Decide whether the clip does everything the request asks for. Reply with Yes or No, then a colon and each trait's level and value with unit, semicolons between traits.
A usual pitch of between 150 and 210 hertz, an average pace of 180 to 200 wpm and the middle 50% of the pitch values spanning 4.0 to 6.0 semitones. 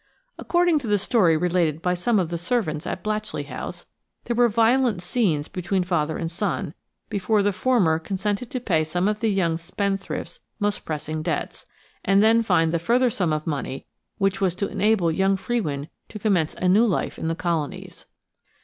Yes: high, 190 Hz; average, 185 wpm; average, 4.7 semitones